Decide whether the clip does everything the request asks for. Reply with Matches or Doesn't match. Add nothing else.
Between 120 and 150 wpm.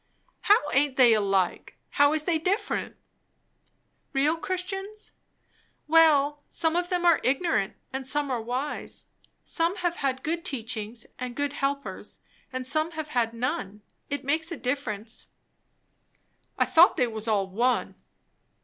Matches